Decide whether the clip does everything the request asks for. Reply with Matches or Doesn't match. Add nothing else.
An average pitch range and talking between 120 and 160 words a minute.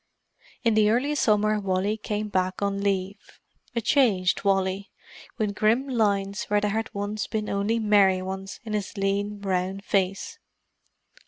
Doesn't match